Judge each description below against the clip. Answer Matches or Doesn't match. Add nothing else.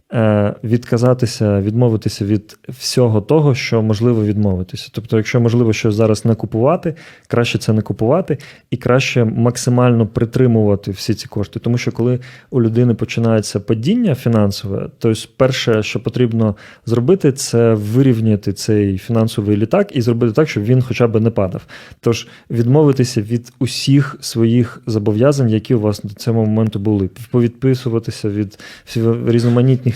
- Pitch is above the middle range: Doesn't match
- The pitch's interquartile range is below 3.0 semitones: Matches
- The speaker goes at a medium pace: Matches